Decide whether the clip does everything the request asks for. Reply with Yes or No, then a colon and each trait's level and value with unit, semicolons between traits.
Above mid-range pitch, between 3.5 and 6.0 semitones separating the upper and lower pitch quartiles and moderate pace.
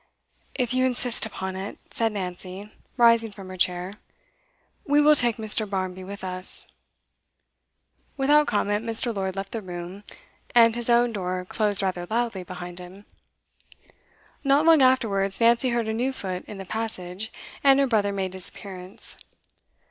Yes: high, 205 Hz; average, 4.1 semitones; average, 155 wpm